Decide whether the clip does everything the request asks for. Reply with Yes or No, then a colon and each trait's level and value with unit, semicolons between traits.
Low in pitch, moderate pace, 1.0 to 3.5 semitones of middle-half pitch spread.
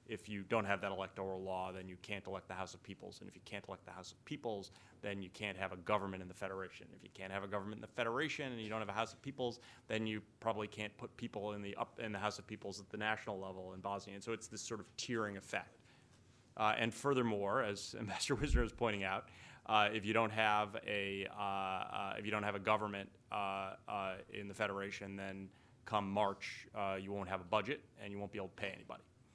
No: low, 105 Hz; fast, 250 wpm; narrow, 2.5 semitones